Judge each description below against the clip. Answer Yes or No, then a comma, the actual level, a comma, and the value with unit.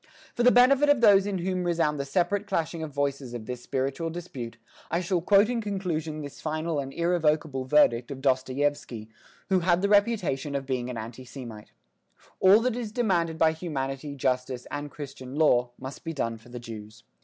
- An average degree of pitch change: No, wide, 5.7 semitones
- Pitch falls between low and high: Yes, medium, 150 Hz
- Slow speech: No, average, 185 wpm